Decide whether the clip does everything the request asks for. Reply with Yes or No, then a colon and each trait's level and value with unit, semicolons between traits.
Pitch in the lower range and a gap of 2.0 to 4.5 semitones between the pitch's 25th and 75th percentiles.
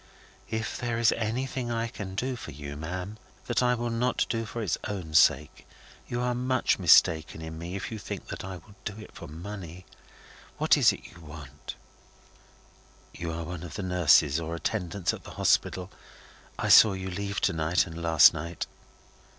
No: very low, 95 Hz; wide, 5.4 semitones